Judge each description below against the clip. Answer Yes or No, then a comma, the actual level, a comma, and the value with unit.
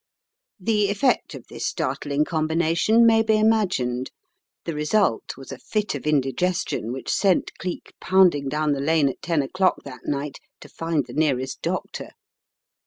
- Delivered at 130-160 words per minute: Yes, average, 155 wpm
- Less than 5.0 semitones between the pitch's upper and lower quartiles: No, wide, 5.4 semitones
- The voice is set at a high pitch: No, medium, 160 Hz